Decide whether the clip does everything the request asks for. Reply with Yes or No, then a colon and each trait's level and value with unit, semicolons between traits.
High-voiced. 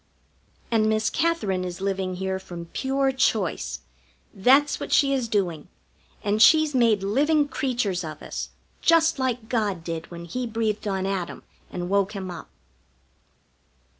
Yes: high, 210 Hz